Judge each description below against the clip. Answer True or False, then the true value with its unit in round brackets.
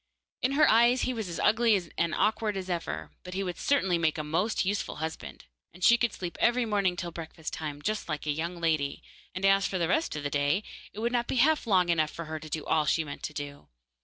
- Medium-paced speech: False (235 wpm)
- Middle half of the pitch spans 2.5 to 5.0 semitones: False (5.6 semitones)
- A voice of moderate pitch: True (180 Hz)